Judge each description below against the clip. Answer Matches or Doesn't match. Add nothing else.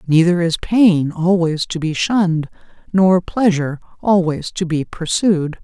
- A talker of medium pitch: Matches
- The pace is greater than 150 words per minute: Doesn't match